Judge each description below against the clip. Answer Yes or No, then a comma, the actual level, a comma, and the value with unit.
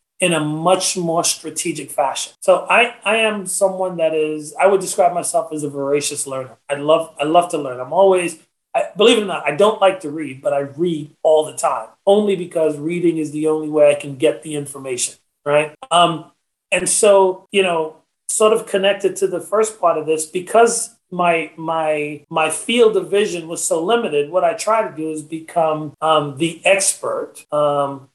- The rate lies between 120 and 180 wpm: No, average, 200 wpm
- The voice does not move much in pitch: No, average, 4.1 semitones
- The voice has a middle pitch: Yes, medium, 165 Hz